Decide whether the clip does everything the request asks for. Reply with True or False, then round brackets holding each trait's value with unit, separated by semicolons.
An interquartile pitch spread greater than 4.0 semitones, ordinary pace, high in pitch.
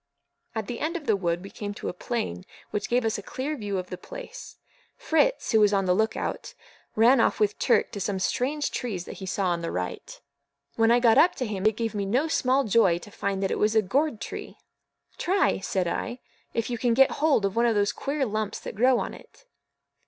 False (4.4 semitones; 235 wpm; 220 Hz)